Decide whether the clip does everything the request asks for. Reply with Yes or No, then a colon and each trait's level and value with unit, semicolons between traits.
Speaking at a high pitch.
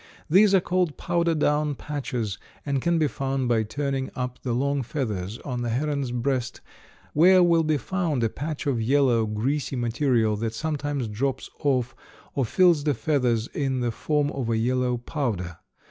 No: low, 135 Hz